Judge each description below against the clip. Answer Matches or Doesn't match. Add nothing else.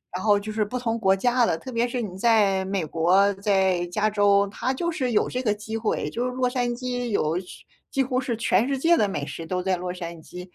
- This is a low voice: Doesn't match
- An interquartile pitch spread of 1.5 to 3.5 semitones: Doesn't match